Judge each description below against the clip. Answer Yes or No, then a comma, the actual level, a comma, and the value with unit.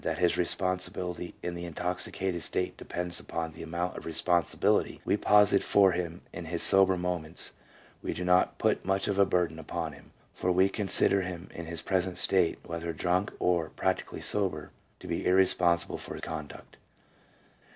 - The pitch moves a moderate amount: No, narrow, 1.7 semitones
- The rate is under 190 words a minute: Yes, average, 170 wpm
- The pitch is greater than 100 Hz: No, very low, 90 Hz